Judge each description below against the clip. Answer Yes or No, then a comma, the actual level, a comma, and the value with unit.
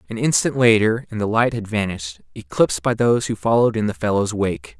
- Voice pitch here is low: Yes, low, 110 Hz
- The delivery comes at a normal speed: No, fast, 215 wpm